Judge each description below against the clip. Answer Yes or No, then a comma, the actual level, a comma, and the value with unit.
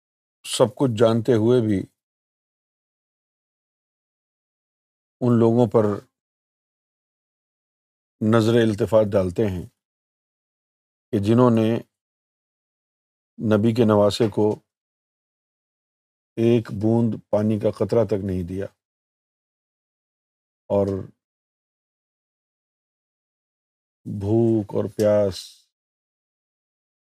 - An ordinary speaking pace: No, slow, 70 wpm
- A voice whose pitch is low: Yes, low, 110 Hz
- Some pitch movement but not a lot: No, narrow, 2.1 semitones